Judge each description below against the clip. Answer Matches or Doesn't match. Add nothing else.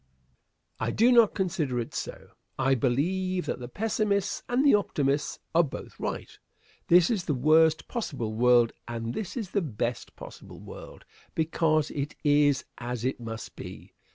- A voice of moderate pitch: Matches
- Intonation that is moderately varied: Doesn't match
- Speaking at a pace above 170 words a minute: Doesn't match